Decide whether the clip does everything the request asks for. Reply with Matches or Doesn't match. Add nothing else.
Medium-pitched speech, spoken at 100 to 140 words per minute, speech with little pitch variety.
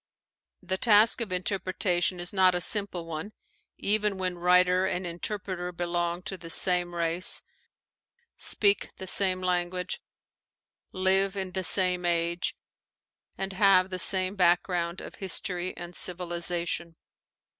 Matches